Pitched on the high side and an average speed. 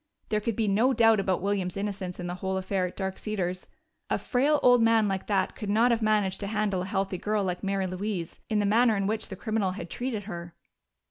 No: high, 200 Hz; fast, 230 wpm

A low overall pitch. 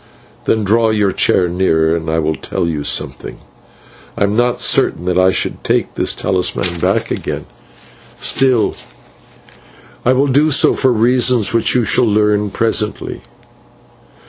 Yes: low, 105 Hz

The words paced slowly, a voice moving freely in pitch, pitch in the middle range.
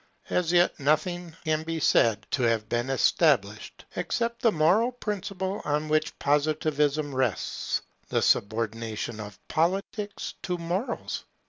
Yes: slow, 125 wpm; wide, 6.6 semitones; medium, 155 Hz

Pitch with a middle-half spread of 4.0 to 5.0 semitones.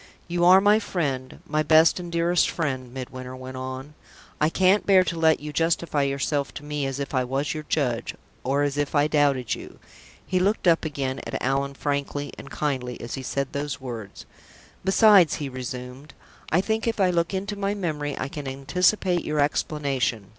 Yes: average, 4.3 semitones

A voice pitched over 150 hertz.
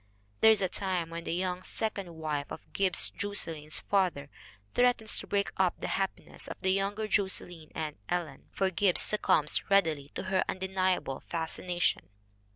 Yes: medium, 185 Hz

